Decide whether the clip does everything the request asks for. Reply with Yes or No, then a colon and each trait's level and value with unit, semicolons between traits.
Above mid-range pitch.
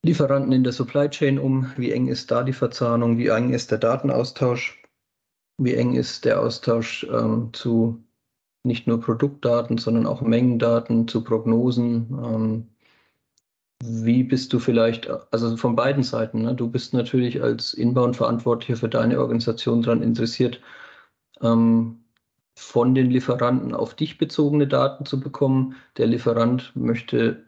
No: low, 120 Hz